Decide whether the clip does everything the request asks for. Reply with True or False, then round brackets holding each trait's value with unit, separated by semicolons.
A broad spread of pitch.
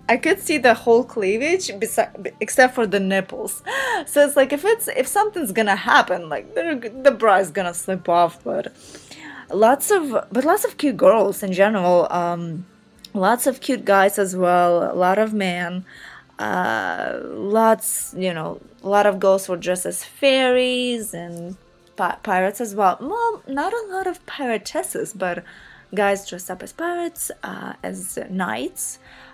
True (7.0 semitones)